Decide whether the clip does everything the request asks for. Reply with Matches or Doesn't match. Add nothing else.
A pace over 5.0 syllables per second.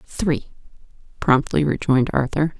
Doesn't match